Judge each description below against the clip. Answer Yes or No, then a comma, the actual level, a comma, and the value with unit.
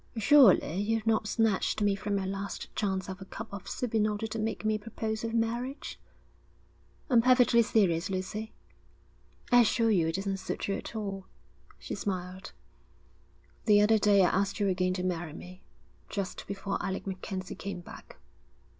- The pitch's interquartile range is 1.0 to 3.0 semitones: Yes, average, 2.7 semitones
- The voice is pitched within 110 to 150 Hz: No, high, 200 Hz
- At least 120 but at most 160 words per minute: No, average, 170 wpm